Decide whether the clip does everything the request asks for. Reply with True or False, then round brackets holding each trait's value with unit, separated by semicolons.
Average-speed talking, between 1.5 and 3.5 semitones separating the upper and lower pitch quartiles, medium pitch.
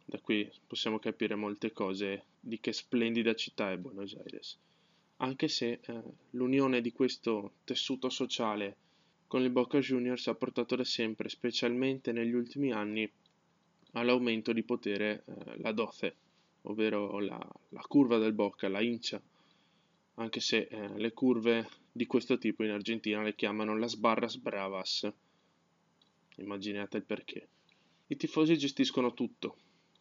False (140 wpm; 3.0 semitones; 115 Hz)